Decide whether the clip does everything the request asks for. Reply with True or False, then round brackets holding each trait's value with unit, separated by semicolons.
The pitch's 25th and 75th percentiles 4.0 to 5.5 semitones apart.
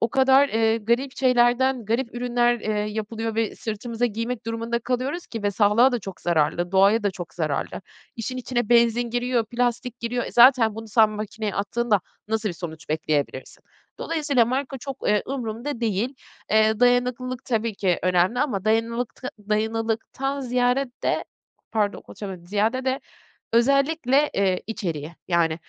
False (3.0 semitones)